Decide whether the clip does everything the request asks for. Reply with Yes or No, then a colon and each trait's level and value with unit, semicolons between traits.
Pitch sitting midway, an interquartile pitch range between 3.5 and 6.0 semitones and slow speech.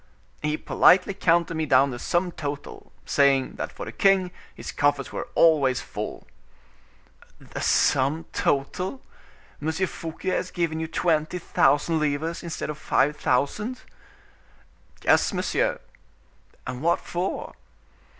Yes: medium, 160 Hz; average, 3.8 semitones; slow, 125 wpm